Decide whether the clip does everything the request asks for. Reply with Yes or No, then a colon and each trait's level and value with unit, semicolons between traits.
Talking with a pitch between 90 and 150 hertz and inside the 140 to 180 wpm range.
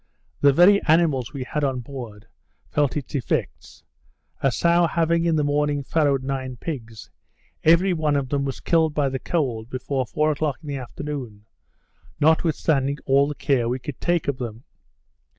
Yes: medium, 140 Hz; average, 170 wpm